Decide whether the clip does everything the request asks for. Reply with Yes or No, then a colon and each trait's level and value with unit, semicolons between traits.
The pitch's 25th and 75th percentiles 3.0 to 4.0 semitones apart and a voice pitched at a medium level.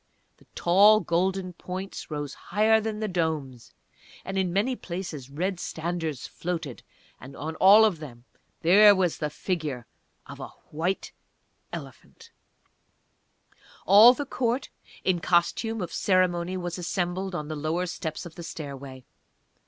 Yes: average, 3.7 semitones; medium, 175 Hz